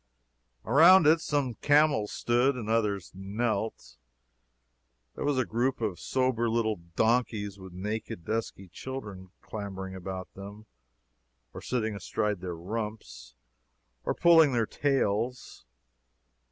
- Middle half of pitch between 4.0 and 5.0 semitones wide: Yes, average, 4.6 semitones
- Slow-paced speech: Yes, slow, 115 wpm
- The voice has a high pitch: No, low, 110 Hz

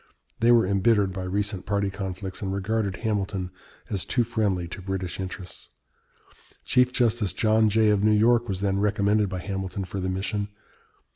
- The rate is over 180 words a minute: No, average, 165 wpm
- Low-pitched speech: Yes, low, 100 Hz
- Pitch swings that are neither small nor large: No, narrow, 2.3 semitones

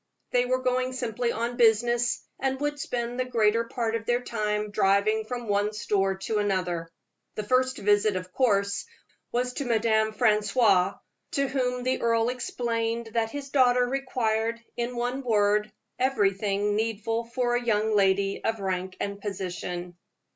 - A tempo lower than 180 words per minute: Yes, average, 155 wpm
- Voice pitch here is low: No, high, 225 Hz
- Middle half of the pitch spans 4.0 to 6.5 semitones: No, average, 3.1 semitones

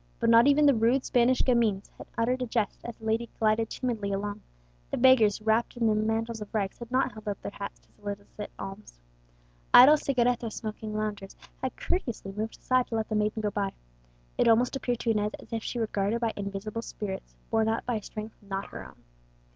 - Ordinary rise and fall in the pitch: No, narrow, 2.3 semitones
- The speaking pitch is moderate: No, high, 220 Hz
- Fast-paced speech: Yes, fast, 210 wpm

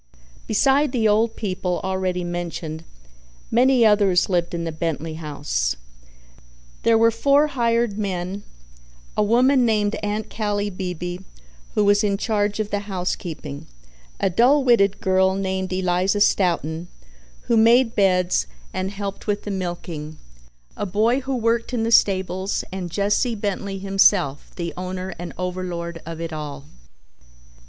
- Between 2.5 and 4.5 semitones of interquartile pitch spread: Yes, average, 3.6 semitones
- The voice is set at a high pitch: Yes, high, 195 Hz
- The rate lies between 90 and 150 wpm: Yes, average, 140 wpm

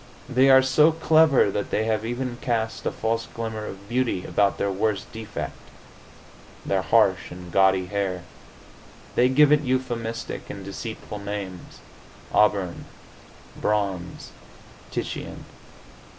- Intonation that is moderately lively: Yes, average, 4.4 semitones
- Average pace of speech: No, slow, 120 wpm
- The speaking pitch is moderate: No, low, 110 Hz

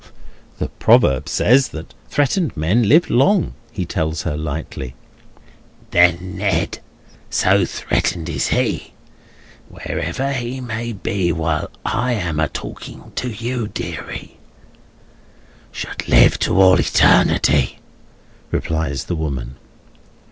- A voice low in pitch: Yes, very low, 90 Hz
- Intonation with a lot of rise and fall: Yes, wide, 7.2 semitones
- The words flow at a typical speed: No, slow, 105 wpm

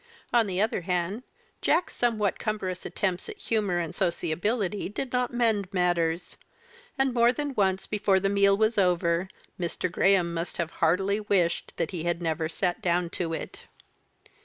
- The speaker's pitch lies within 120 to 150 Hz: No, high, 190 Hz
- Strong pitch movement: No, average, 3.7 semitones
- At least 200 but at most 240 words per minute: No, average, 160 wpm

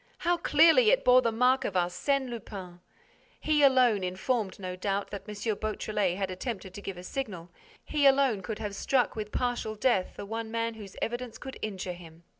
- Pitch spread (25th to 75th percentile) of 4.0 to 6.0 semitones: Yes, average, 5.1 semitones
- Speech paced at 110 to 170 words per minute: No, average, 190 wpm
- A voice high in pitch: Yes, high, 215 Hz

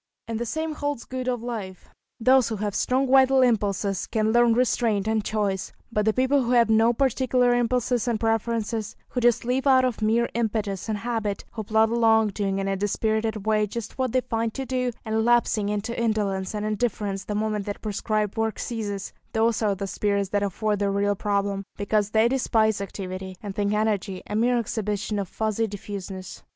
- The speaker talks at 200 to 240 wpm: No, average, 190 wpm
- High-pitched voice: Yes, high, 220 Hz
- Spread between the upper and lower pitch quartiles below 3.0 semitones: Yes, narrow, 2.6 semitones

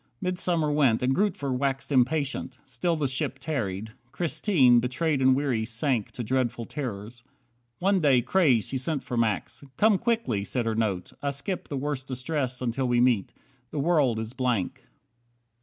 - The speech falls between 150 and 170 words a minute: Yes, average, 160 wpm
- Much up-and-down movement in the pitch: No, average, 3.8 semitones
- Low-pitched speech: Yes, low, 130 Hz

